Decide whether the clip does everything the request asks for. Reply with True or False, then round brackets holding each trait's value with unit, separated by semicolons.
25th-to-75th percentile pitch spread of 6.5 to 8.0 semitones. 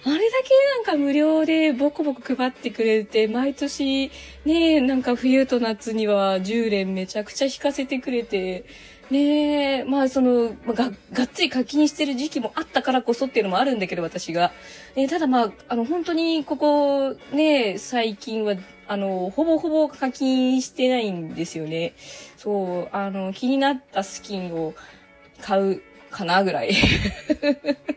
False (5.4 semitones)